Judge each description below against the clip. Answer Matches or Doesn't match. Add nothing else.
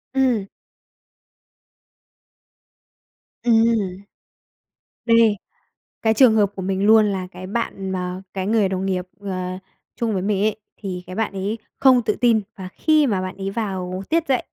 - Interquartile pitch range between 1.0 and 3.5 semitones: Matches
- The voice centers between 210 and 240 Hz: Doesn't match